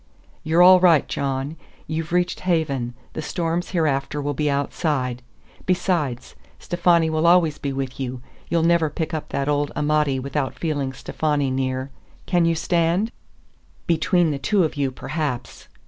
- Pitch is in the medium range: Yes, medium, 155 Hz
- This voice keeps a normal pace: Yes, average, 150 wpm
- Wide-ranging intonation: No, average, 3.6 semitones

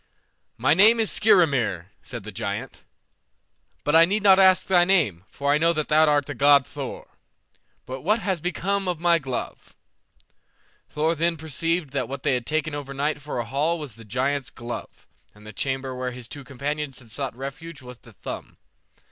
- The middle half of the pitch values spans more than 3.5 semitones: Yes, average, 4.6 semitones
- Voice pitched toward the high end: No, medium, 145 Hz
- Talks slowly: No, average, 185 wpm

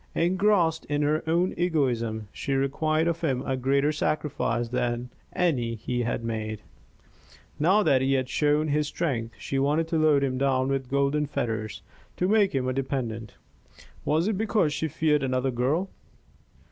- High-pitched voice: No, medium, 140 Hz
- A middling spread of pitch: Yes, average, 3.9 semitones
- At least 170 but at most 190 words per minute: No, average, 160 wpm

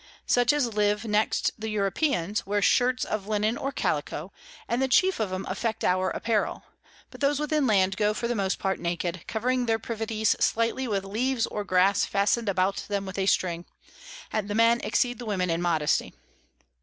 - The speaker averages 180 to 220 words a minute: Yes, average, 185 wpm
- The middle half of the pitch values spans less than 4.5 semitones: Yes, average, 3.5 semitones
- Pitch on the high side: Yes, high, 210 Hz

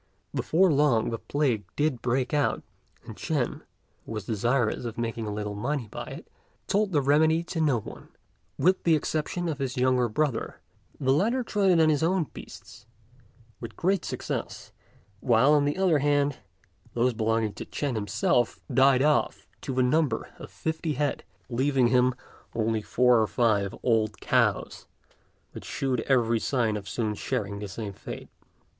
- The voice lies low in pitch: Yes, low, 130 Hz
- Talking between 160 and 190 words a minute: Yes, average, 165 wpm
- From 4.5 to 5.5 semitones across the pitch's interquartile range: Yes, average, 4.9 semitones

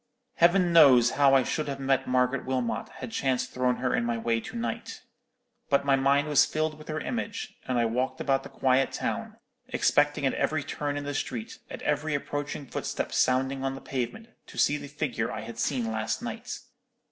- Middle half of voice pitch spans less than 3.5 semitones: Yes, narrow, 2.5 semitones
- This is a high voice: No, low, 135 Hz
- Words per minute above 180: Yes, average, 200 wpm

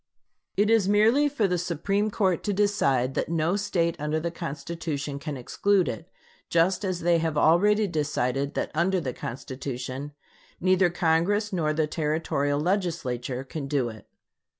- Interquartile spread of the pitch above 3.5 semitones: Yes, average, 5.1 semitones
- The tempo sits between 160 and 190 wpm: No, average, 150 wpm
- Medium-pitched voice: Yes, medium, 165 Hz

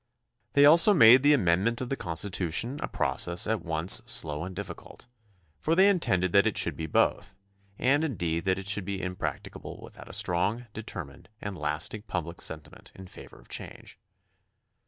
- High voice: No, very low, 95 Hz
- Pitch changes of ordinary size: No, wide, 5.7 semitones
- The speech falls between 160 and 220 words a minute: Yes, average, 175 wpm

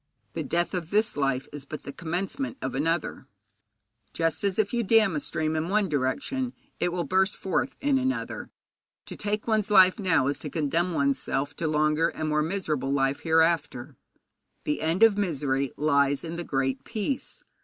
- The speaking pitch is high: No, medium, 165 Hz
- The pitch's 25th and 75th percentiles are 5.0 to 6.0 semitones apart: Yes, wide, 5.5 semitones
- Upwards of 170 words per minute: Yes, average, 180 wpm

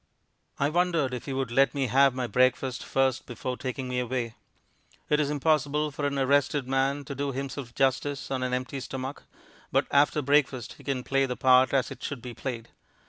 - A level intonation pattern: Yes, narrow, 1.8 semitones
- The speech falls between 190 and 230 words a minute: Yes, average, 195 wpm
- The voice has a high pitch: No, low, 135 Hz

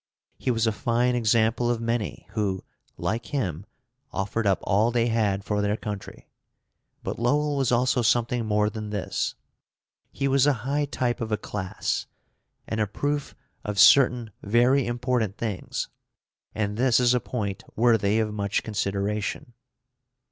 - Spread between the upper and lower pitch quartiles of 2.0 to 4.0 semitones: Yes, average, 2.9 semitones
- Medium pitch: No, low, 115 Hz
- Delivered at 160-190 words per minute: No, average, 150 wpm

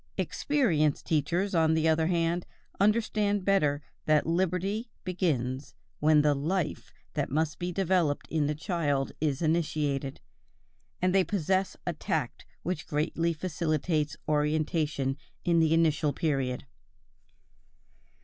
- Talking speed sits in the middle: No, slow, 120 wpm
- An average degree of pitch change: Yes, average, 3.4 semitones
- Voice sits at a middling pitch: Yes, medium, 160 Hz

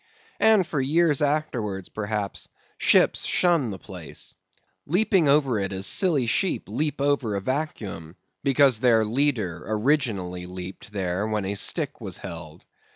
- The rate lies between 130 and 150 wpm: Yes, average, 145 wpm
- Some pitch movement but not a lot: No, wide, 7.1 semitones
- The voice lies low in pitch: Yes, low, 115 Hz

